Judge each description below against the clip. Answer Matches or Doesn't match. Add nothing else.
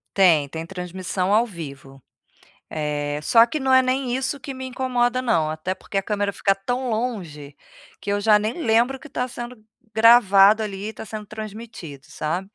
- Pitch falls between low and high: Doesn't match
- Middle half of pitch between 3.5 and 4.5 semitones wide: Doesn't match